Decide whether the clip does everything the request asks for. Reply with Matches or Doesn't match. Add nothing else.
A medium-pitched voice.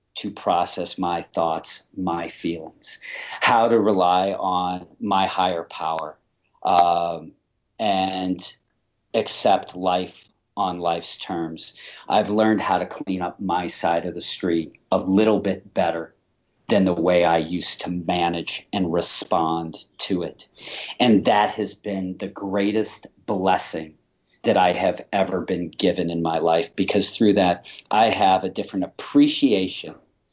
Doesn't match